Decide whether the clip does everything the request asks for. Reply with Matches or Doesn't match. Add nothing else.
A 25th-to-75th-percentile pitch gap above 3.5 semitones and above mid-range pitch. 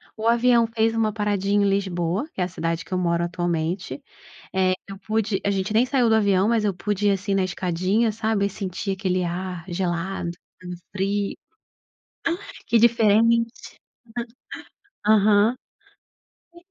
Doesn't match